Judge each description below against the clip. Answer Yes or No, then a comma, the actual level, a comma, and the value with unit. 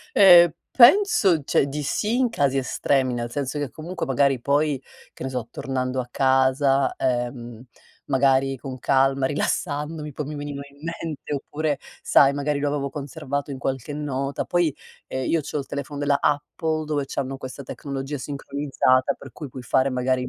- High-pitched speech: No, medium, 140 Hz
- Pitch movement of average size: No, narrow, 2.0 semitones